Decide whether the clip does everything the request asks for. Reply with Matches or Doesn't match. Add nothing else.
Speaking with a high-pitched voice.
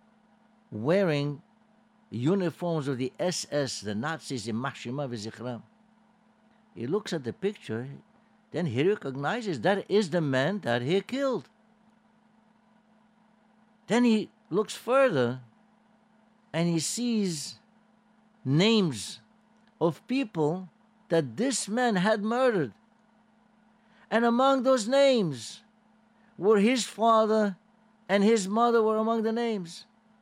Matches